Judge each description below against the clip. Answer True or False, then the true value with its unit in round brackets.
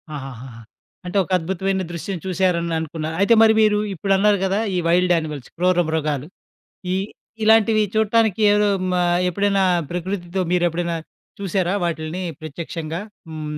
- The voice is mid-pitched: True (180 Hz)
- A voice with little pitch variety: False (3.5 semitones)